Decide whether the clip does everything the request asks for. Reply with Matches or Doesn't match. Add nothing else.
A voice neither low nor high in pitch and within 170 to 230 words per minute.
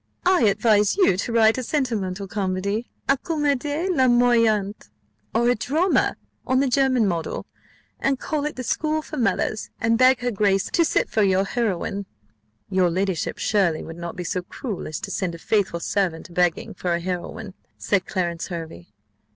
Doesn't match